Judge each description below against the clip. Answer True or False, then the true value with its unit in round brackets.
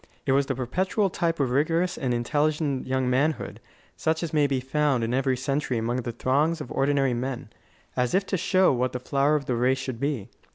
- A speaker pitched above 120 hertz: True (135 Hz)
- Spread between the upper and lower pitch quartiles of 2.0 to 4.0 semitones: True (3.2 semitones)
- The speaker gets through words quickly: True (210 wpm)